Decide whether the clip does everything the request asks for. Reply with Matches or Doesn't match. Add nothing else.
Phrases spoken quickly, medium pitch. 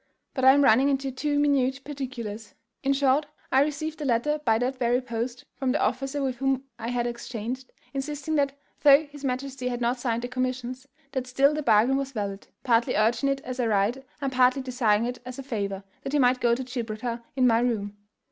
Doesn't match